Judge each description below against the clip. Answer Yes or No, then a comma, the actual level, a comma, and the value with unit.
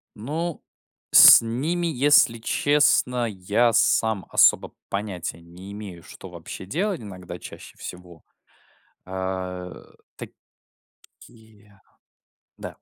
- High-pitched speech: No, low, 105 Hz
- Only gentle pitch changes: No, wide, 5.4 semitones